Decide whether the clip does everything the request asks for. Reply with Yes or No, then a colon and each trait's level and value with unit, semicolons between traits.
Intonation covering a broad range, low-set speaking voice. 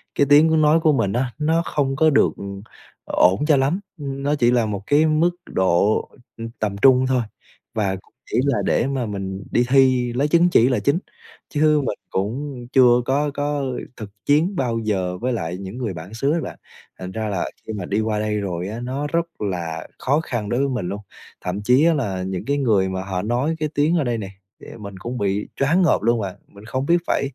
Yes: wide, 6.2 semitones; low, 120 Hz